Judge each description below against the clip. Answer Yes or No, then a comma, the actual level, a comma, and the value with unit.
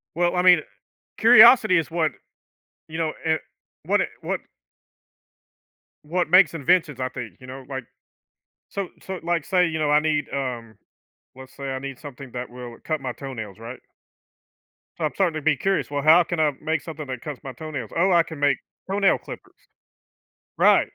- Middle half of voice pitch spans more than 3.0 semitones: Yes, average, 4.7 semitones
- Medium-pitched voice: Yes, medium, 155 Hz